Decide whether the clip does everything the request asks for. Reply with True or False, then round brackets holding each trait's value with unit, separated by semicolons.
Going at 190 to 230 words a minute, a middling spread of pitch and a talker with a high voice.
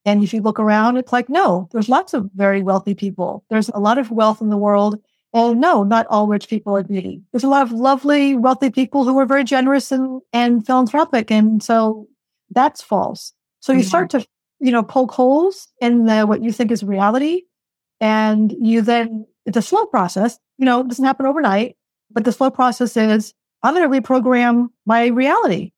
True (205 wpm; 3.6 semitones; 235 Hz)